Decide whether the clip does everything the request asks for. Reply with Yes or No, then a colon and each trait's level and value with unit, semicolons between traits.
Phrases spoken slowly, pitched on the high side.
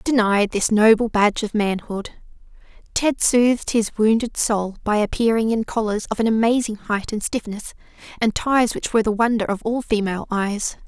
No: average, 170 wpm; high, 220 Hz